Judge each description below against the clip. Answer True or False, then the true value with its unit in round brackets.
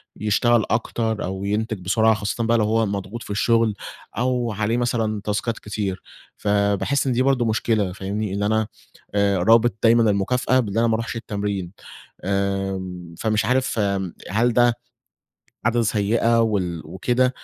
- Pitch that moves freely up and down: False (2.7 semitones)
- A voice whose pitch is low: True (110 Hz)